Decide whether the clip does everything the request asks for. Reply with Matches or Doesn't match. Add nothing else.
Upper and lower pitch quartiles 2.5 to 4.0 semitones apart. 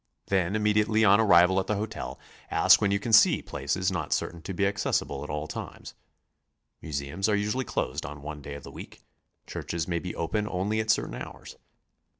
Doesn't match